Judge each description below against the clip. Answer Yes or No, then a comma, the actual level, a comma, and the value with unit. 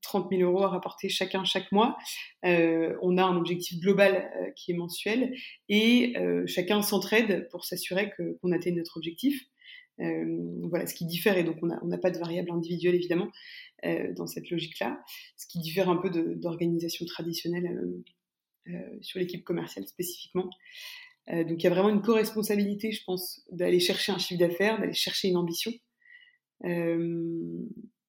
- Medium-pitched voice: Yes, medium, 180 Hz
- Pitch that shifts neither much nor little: Yes, average, 3.9 semitones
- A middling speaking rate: Yes, average, 175 wpm